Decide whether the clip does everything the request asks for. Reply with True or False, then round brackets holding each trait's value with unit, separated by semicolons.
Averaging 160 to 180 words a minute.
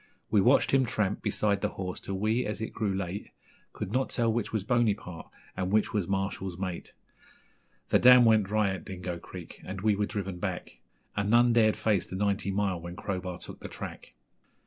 False (195 wpm)